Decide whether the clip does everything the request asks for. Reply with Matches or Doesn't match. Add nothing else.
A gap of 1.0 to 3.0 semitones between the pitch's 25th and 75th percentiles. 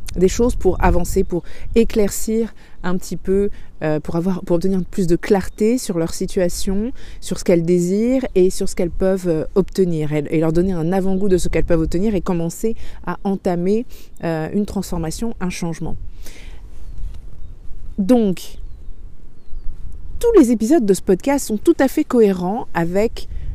Doesn't match